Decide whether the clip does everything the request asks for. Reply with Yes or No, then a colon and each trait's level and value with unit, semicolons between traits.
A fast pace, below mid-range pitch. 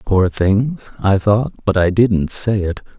No: average, 180 wpm; low, 100 Hz